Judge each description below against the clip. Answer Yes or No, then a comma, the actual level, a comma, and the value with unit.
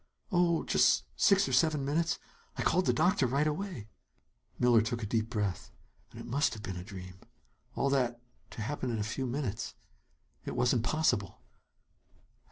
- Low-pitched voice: Yes, low, 125 Hz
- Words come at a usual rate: Yes, average, 170 wpm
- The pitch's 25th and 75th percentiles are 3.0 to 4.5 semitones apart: No, wide, 5.6 semitones